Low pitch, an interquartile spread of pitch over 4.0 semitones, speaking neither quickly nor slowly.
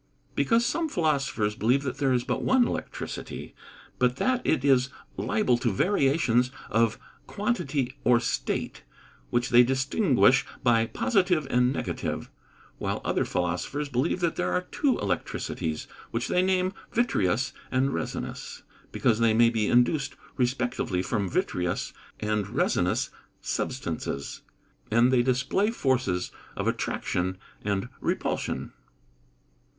No: low, 125 Hz; average, 5.3 semitones; slow, 125 wpm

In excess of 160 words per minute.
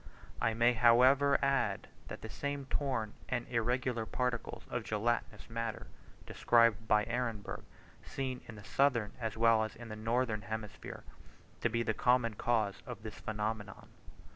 No: average, 150 wpm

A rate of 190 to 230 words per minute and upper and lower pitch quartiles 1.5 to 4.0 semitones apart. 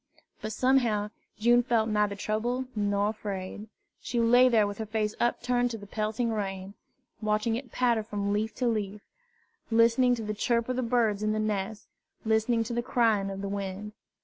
No: average, 180 wpm; narrow, 2.4 semitones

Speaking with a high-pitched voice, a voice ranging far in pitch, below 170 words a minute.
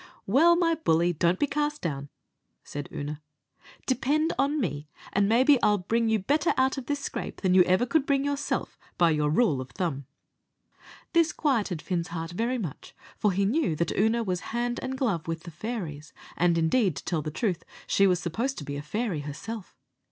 No: high, 200 Hz; wide, 8.0 semitones; average, 195 wpm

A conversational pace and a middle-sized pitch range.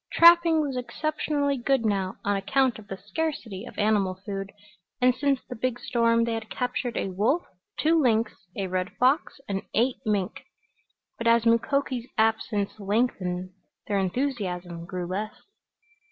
Yes: average, 150 wpm; average, 4.7 semitones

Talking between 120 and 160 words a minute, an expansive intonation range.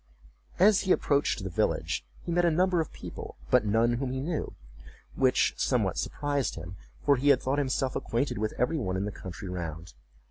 No: average, 190 wpm; wide, 6.2 semitones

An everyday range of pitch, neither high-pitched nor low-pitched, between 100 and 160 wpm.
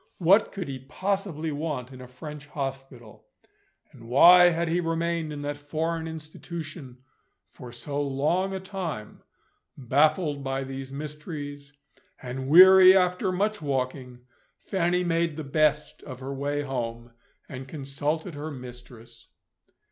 Yes: average, 4.0 semitones; medium, 145 Hz; slow, 135 wpm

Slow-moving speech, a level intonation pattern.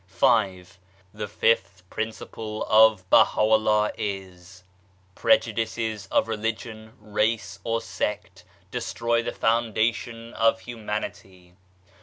Yes: slow, 90 wpm; narrow, 2.3 semitones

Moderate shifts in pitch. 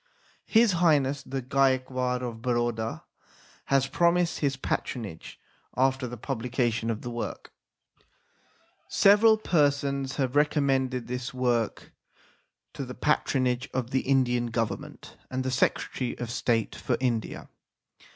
No: narrow, 2.3 semitones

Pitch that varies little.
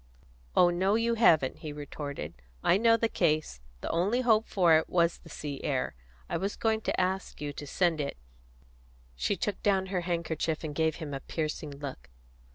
No: average, 4.8 semitones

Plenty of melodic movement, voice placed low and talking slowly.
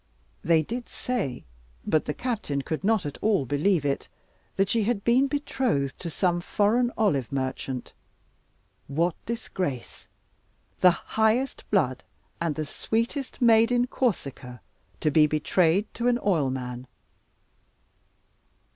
No: wide, 8.2 semitones; medium, 180 Hz; slow, 125 wpm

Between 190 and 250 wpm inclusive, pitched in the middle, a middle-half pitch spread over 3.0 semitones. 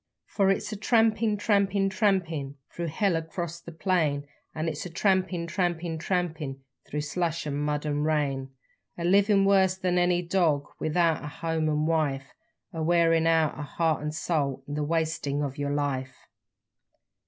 No: average, 170 wpm; medium, 165 Hz; average, 3.5 semitones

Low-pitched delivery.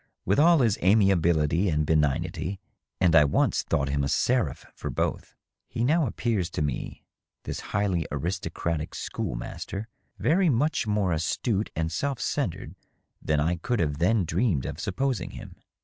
Yes: very low, 90 Hz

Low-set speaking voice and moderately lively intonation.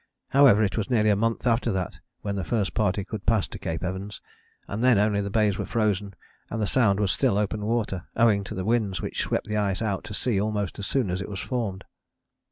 No: low, 105 Hz; narrow, 2.3 semitones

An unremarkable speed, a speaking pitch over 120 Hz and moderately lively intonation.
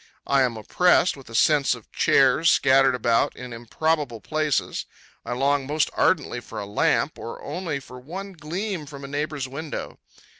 Yes: average, 165 wpm; medium, 140 Hz; average, 3.7 semitones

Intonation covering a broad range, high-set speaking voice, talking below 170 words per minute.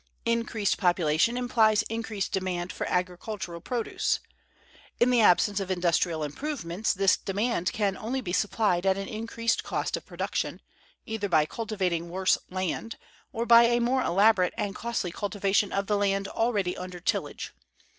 No: average, 3.8 semitones; high, 200 Hz; average, 150 wpm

